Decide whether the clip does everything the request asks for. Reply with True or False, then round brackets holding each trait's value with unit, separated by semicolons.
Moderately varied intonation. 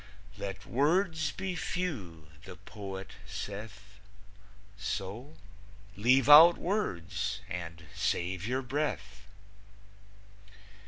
False (7.5 semitones)